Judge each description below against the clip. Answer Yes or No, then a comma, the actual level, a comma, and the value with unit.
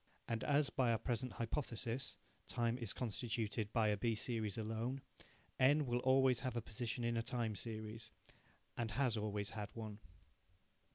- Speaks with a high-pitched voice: No, low, 115 Hz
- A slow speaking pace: No, average, 160 wpm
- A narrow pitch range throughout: Yes, narrow, 2.3 semitones